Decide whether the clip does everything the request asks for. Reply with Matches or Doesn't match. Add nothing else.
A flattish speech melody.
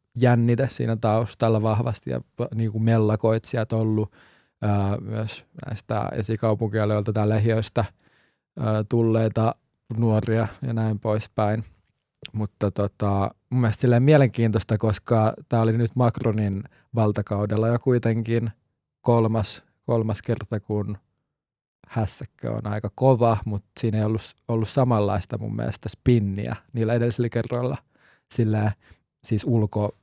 Matches